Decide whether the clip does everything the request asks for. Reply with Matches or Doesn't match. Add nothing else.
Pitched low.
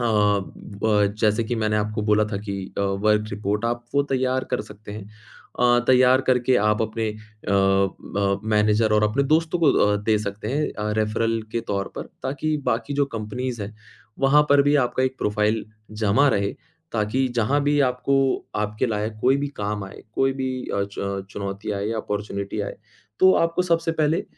Matches